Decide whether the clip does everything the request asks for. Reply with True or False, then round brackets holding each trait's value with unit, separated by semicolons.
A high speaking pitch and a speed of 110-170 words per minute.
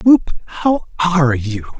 False (170 Hz; 135 wpm)